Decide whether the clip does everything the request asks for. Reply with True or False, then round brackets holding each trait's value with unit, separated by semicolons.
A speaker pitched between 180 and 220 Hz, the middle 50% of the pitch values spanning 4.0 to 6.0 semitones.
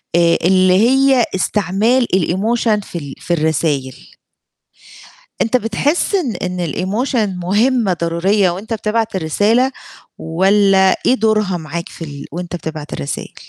True (190 Hz; 4.7 semitones)